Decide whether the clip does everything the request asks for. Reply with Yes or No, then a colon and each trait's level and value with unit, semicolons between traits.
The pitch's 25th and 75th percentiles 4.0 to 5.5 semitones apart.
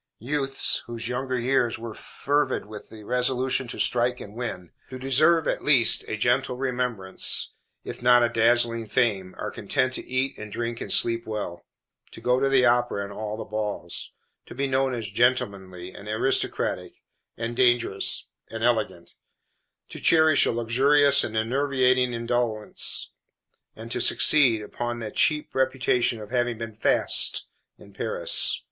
No: average, 2.8 semitones